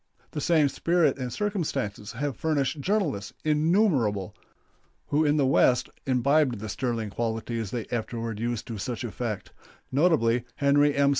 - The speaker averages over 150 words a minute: No, average, 140 wpm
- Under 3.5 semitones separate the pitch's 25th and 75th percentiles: No, average, 4.6 semitones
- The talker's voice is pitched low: Yes, low, 130 Hz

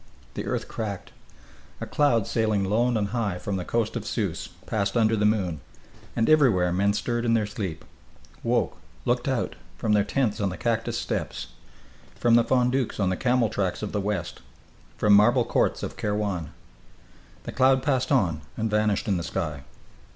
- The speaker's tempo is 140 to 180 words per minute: Yes, average, 175 wpm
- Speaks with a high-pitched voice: No, low, 105 Hz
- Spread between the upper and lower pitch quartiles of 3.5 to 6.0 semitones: No, average, 3.1 semitones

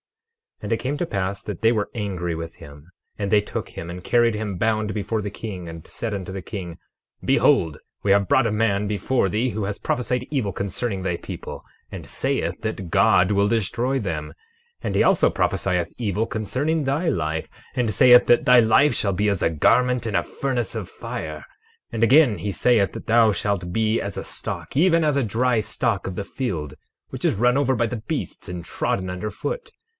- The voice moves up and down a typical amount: Yes, average, 4.3 semitones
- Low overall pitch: Yes, low, 105 Hz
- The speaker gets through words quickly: Yes, fast, 210 wpm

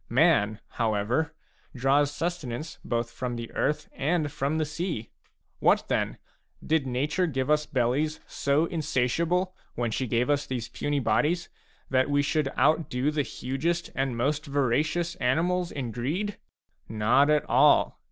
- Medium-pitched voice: Yes, medium, 145 Hz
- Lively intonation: No, average, 4.2 semitones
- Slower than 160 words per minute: Yes, average, 145 wpm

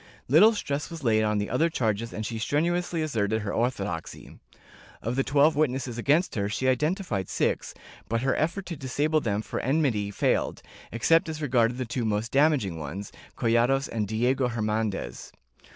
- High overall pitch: No, low, 125 Hz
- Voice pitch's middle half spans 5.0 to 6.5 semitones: Yes, wide, 5.5 semitones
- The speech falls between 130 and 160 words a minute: No, average, 170 wpm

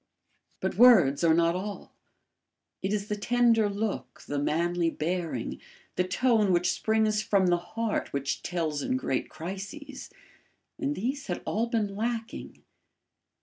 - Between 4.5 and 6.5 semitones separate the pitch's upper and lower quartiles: Yes, average, 4.8 semitones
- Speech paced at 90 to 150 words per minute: Yes, average, 140 wpm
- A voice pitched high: Yes, high, 200 Hz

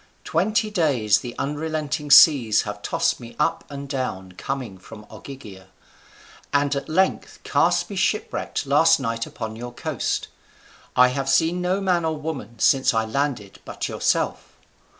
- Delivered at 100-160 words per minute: Yes, average, 150 wpm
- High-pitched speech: No, low, 135 Hz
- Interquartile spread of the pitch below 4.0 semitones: No, wide, 5.6 semitones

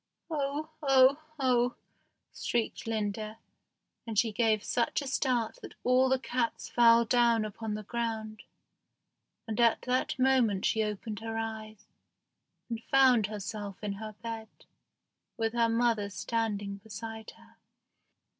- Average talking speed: No, slow, 130 wpm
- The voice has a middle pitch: No, high, 225 Hz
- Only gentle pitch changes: Yes, narrow, 2.1 semitones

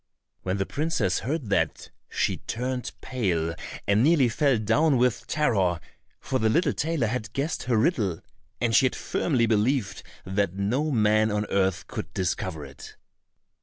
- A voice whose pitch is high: No, low, 115 Hz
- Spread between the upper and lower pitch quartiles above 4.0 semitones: Yes, average, 5.2 semitones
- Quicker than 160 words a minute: No, average, 155 wpm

